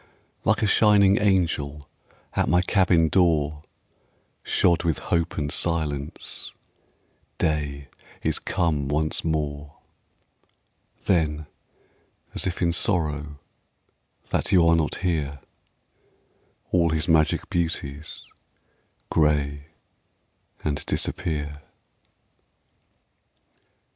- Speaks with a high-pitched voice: No, very low, 80 Hz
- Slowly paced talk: Yes, slow, 90 wpm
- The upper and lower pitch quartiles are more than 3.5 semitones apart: No, average, 2.8 semitones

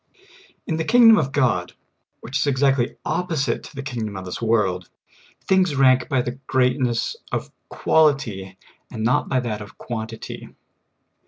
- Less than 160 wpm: Yes, average, 150 wpm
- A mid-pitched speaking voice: No, low, 125 Hz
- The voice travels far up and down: No, average, 4.2 semitones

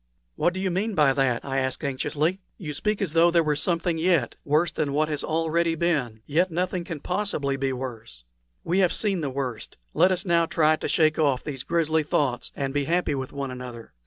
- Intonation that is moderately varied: Yes, average, 4.0 semitones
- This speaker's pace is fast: Yes, fast, 215 wpm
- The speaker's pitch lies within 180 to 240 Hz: No, medium, 155 Hz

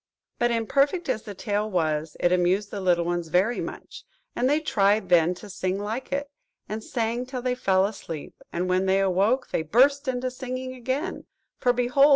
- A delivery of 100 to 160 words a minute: No, average, 190 wpm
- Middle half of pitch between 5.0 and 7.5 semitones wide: Yes, wide, 5.6 semitones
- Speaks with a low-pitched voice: No, high, 215 Hz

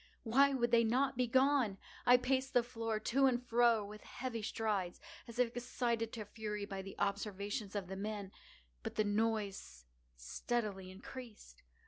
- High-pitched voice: Yes, high, 225 Hz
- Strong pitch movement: No, average, 3.3 semitones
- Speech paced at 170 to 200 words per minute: No, average, 155 wpm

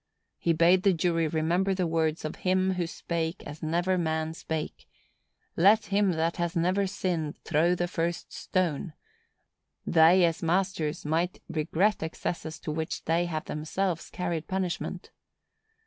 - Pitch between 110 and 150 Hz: No, medium, 170 Hz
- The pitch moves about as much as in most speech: No, narrow, 2.3 semitones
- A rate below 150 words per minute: Yes, average, 140 wpm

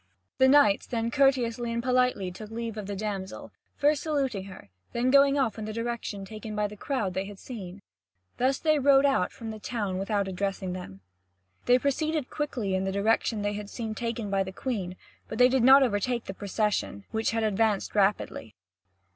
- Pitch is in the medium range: No, high, 220 Hz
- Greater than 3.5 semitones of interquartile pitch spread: Yes, average, 4.2 semitones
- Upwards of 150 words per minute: Yes, average, 195 wpm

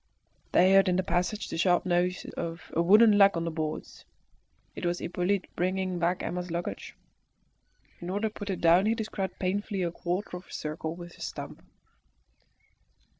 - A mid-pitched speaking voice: Yes, medium, 180 Hz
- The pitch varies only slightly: Yes, narrow, 2.1 semitones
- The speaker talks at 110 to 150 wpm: No, average, 175 wpm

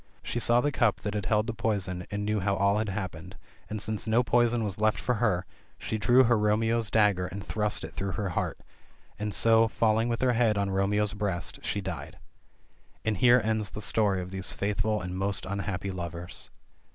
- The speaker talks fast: Yes, fast, 210 wpm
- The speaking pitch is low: Yes, low, 105 Hz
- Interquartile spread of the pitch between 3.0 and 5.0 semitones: No, narrow, 2.5 semitones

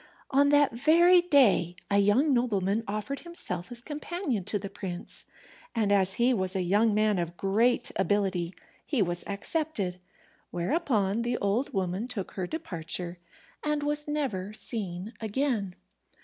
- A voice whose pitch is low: No, high, 210 Hz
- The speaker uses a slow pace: No, average, 145 wpm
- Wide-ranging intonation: Yes, wide, 6.3 semitones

